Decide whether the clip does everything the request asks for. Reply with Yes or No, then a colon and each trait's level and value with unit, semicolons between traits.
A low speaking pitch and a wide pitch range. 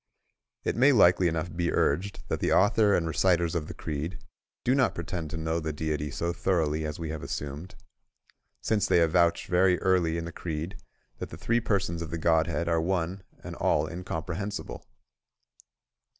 No: very low, 85 Hz; narrow, 2.5 semitones